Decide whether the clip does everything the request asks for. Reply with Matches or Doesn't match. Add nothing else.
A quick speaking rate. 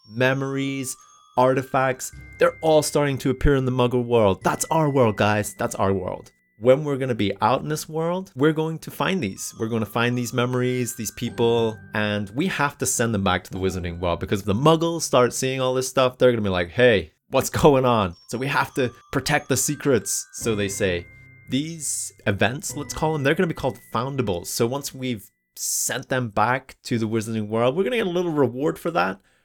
Matches